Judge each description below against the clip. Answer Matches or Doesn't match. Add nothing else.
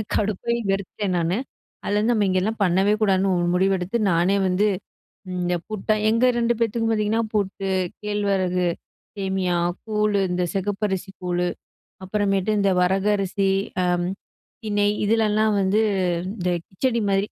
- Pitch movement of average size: Doesn't match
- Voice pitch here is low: Doesn't match